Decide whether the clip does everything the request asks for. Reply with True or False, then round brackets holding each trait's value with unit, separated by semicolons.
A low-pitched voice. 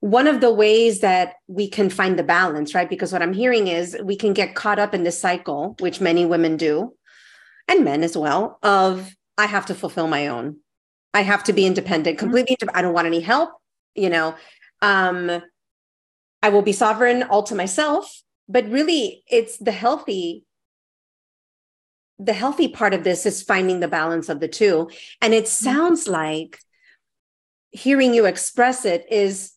False (195 Hz)